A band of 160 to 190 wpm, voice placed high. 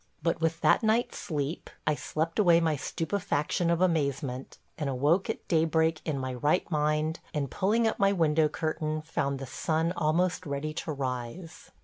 No: average, 165 wpm; medium, 155 Hz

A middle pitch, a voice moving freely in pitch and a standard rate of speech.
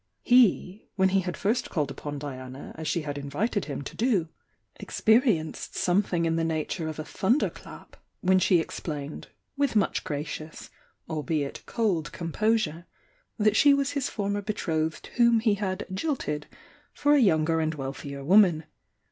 Yes: medium, 175 Hz; wide, 5.7 semitones; average, 160 wpm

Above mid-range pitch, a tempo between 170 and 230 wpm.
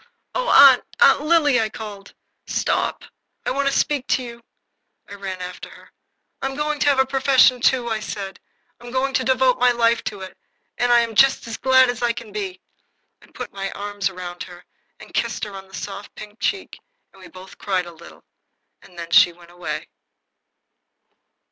Yes: high, 230 Hz; average, 190 wpm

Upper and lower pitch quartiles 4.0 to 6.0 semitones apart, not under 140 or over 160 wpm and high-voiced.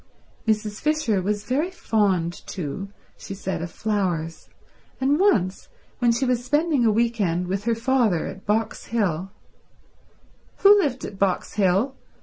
Yes: average, 4.9 semitones; average, 145 wpm; high, 215 Hz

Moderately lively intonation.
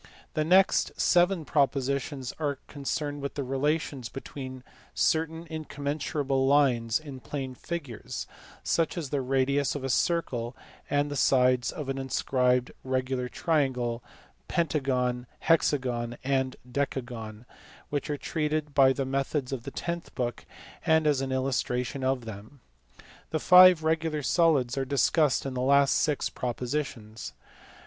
Yes: average, 3.0 semitones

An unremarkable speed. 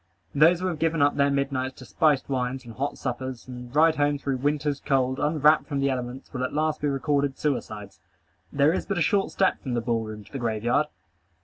No: fast, 225 wpm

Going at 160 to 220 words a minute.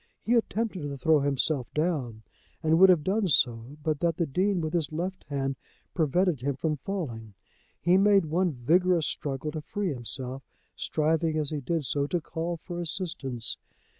Yes: average, 170 wpm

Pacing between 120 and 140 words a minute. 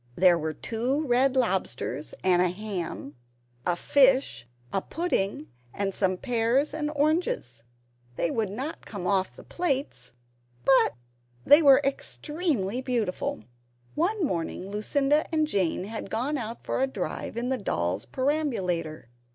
Yes: slow, 135 wpm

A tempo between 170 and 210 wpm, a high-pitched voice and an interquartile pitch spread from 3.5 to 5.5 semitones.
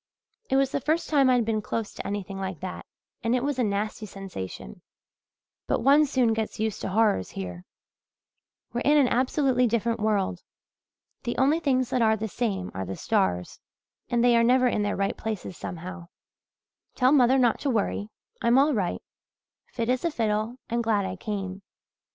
Yes: average, 180 wpm; high, 225 Hz; average, 4.4 semitones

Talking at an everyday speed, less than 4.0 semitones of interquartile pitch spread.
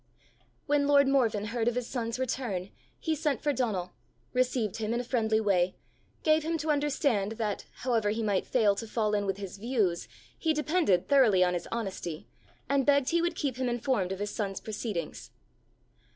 No: average, 185 wpm; average, 5.1 semitones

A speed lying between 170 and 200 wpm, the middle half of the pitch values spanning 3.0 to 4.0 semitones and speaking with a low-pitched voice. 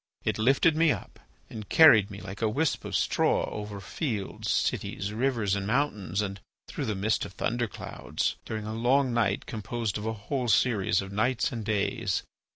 Yes: average, 180 wpm; average, 3.4 semitones; low, 110 Hz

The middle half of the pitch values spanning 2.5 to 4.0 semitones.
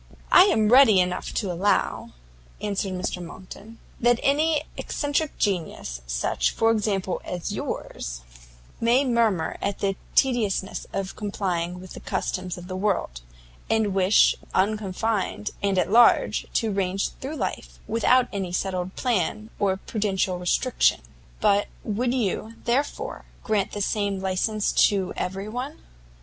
Yes: average, 3.5 semitones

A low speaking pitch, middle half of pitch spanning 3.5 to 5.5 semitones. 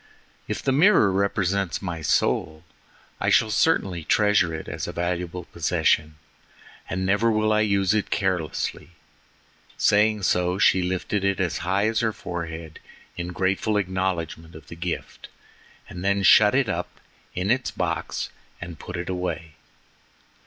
No: very low, 95 Hz; average, 3.1 semitones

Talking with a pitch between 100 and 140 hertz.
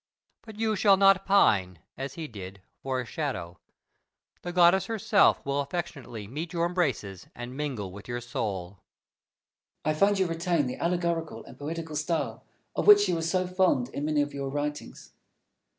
No: medium, 150 Hz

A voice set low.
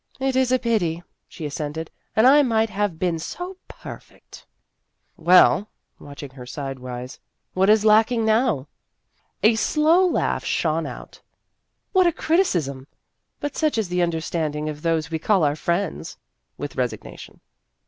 No: medium, 180 Hz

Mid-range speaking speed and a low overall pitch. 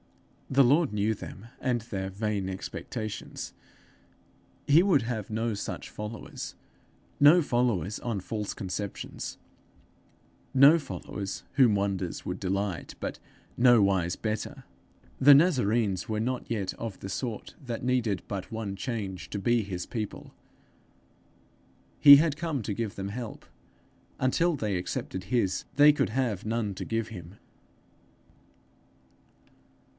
No: slow, 125 wpm; low, 110 Hz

